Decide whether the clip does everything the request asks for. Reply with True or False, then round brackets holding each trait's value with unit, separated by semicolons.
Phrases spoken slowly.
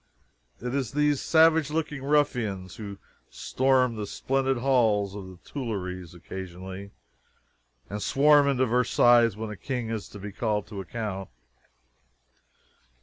True (130 wpm)